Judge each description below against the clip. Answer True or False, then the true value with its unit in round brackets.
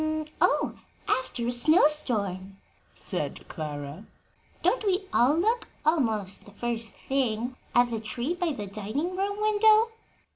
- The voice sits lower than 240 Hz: False (245 Hz)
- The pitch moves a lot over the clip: True (8.6 semitones)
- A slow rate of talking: True (130 wpm)